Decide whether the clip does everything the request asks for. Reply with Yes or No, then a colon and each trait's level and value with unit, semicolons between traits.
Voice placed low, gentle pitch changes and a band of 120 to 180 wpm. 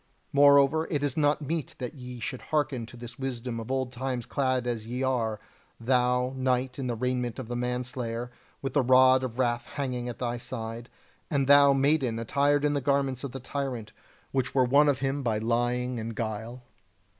No: low, 125 Hz; narrow, 2.2 semitones; average, 190 wpm